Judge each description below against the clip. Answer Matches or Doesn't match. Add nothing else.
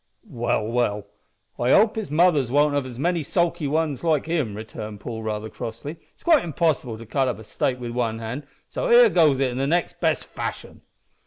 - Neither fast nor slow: Matches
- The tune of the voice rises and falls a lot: Matches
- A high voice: Doesn't match